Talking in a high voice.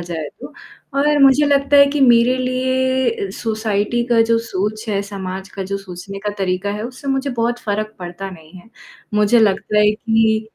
Yes: high, 220 Hz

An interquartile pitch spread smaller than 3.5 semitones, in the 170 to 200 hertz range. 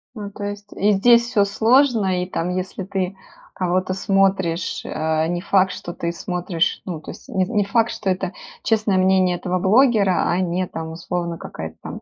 Yes: narrow, 2.4 semitones; medium, 185 Hz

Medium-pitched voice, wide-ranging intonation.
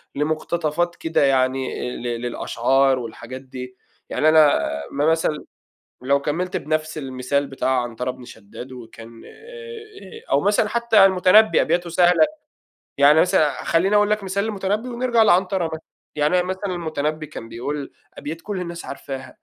Yes: medium, 155 Hz; wide, 6.0 semitones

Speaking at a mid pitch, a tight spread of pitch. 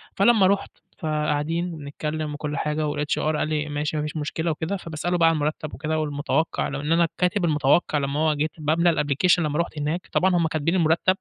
Yes: medium, 155 Hz; narrow, 2.1 semitones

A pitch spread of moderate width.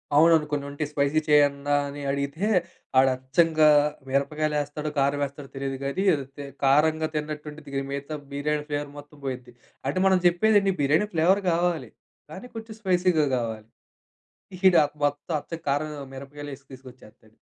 No: narrow, 2.2 semitones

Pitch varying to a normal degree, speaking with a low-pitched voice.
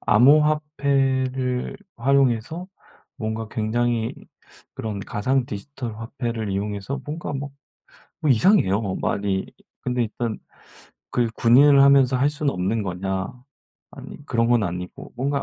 Yes: average, 4.4 semitones; low, 120 Hz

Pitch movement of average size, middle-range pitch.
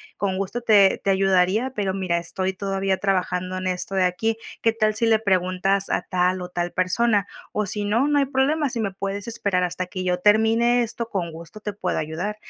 No: average, 3.3 semitones; high, 195 Hz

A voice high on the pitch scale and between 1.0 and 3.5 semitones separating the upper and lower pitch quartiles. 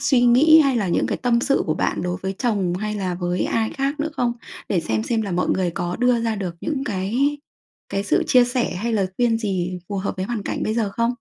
No: high, 220 Hz; average, 4.8 semitones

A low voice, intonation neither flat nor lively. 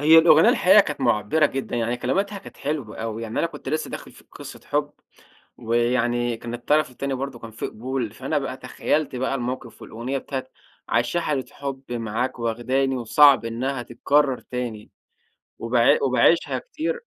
Yes: low, 130 Hz; average, 3.5 semitones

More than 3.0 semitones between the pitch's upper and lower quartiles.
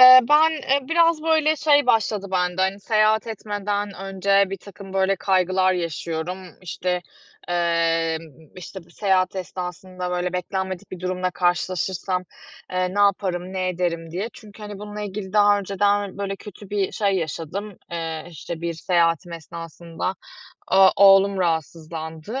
No: narrow, 2.6 semitones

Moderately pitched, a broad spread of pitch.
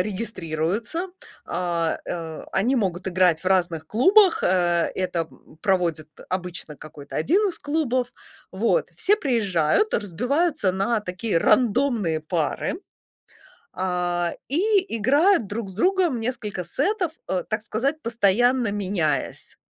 No: high, 205 Hz; wide, 6.9 semitones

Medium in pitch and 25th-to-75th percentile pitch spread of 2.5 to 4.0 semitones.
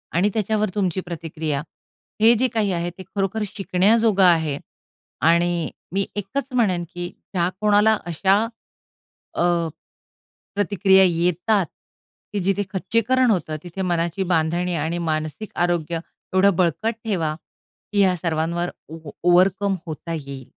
Yes: medium, 180 Hz; average, 3.3 semitones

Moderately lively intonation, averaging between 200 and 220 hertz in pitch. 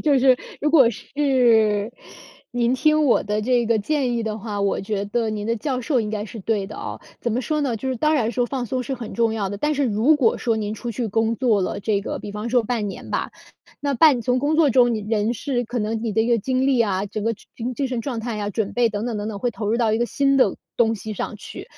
No: average, 3.1 semitones; high, 230 Hz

